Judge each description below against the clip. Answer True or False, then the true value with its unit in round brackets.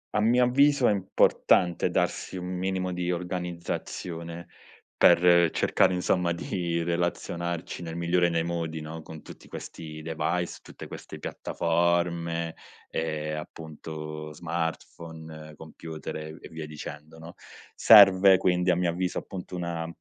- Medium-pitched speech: False (85 Hz)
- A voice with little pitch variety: True (1.8 semitones)